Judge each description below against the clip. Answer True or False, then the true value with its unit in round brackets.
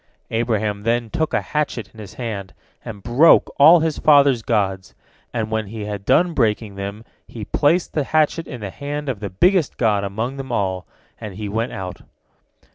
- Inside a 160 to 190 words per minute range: True (185 wpm)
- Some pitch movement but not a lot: False (5.7 semitones)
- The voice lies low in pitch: True (115 Hz)